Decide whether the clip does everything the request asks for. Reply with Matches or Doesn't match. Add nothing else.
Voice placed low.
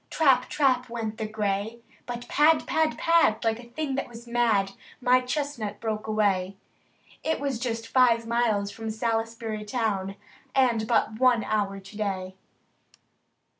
Doesn't match